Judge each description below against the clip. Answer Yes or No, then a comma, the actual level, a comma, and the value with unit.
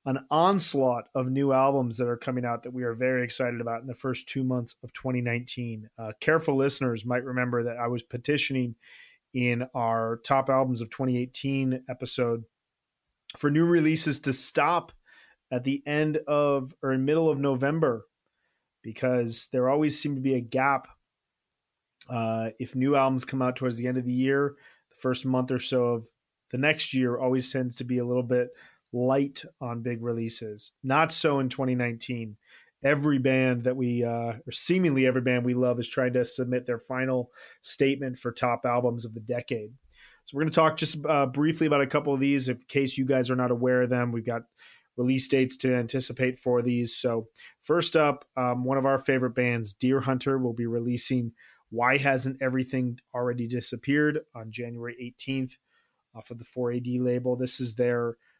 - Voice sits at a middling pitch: No, low, 125 Hz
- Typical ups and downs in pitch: No, narrow, 1.9 semitones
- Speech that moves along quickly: No, average, 185 wpm